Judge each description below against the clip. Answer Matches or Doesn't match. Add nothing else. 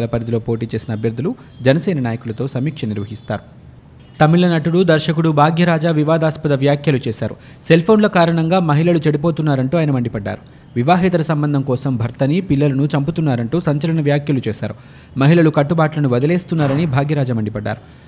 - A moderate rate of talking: Matches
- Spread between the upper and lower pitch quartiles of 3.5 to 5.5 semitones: Matches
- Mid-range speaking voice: Matches